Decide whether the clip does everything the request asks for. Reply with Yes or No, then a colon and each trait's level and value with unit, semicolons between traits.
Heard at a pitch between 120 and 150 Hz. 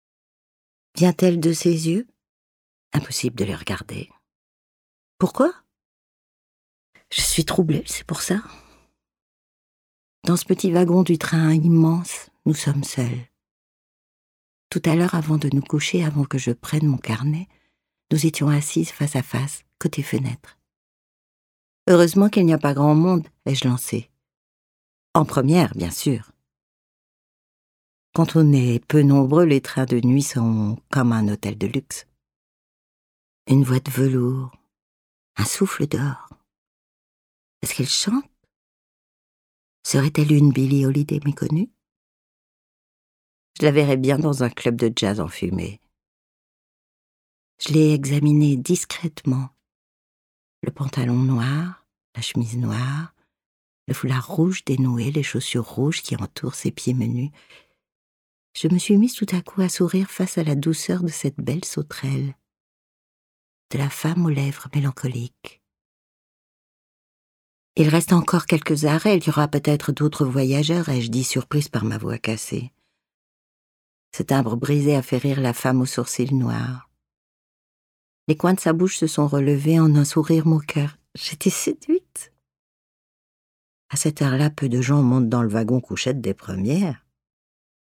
Yes: medium, 140 Hz